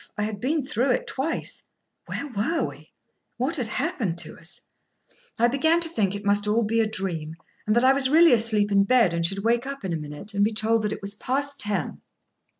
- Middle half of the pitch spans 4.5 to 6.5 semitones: Yes, average, 4.9 semitones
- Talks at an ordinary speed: No, fast, 220 wpm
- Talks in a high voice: Yes, high, 220 Hz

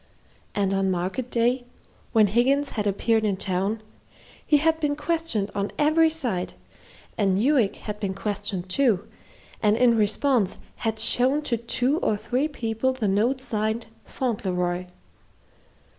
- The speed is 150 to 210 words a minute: No, average, 140 wpm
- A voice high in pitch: Yes, high, 225 Hz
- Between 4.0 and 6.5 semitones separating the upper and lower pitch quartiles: Yes, average, 4.5 semitones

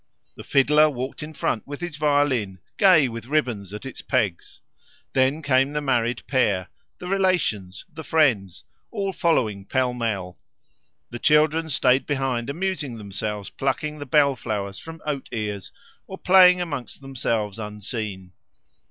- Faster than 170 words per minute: No, average, 145 wpm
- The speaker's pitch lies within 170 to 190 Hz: No, low, 130 Hz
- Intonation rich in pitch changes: Yes, wide, 6.0 semitones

